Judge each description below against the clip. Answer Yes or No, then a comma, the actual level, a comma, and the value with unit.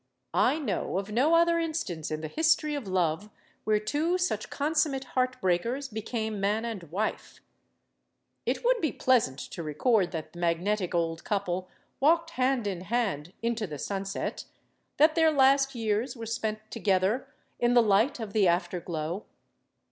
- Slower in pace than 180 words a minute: Yes, average, 160 wpm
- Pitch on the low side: No, high, 220 Hz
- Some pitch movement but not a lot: No, wide, 6.6 semitones